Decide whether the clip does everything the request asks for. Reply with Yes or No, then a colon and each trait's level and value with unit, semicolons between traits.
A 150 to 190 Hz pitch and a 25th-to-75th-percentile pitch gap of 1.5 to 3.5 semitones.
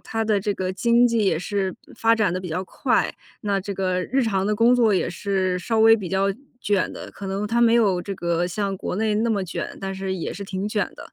No: high, 200 Hz; average, 2.8 semitones